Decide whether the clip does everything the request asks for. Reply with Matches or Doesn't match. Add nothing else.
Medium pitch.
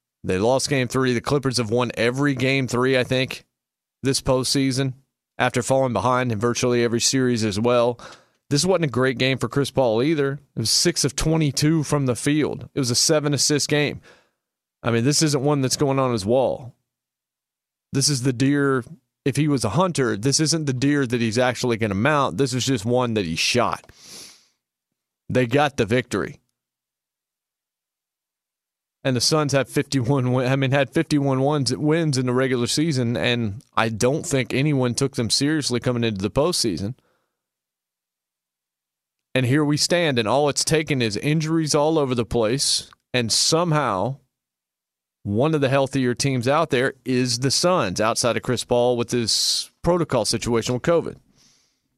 Doesn't match